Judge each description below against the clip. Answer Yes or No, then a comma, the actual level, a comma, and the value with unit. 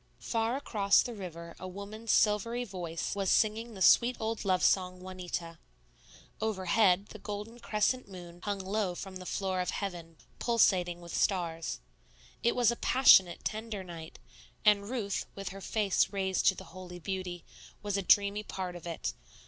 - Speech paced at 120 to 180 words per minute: Yes, average, 165 wpm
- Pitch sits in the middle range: No, high, 195 Hz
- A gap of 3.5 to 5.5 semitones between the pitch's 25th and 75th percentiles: No, average, 3.1 semitones